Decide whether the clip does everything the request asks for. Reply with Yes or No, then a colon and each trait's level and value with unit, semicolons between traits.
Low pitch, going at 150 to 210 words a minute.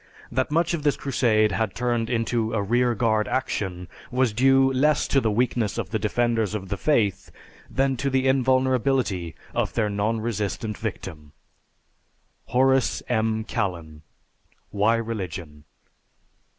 No: low, 115 Hz; slow, 135 wpm